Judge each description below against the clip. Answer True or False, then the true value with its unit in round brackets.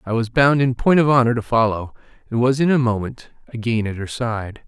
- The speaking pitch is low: True (120 Hz)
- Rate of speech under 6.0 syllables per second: True (5.4 syllables/s)